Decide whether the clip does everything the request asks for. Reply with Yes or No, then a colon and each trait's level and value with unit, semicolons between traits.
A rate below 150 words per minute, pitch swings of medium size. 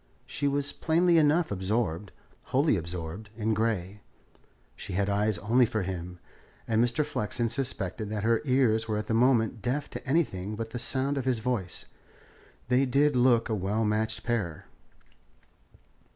No: average, 155 wpm; average, 4.1 semitones